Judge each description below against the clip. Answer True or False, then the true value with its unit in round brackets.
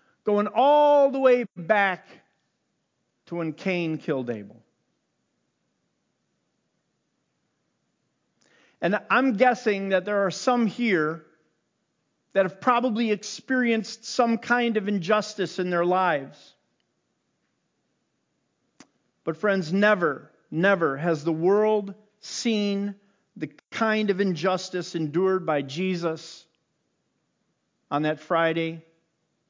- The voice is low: False (195 Hz)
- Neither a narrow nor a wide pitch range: True (4.5 semitones)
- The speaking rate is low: True (95 wpm)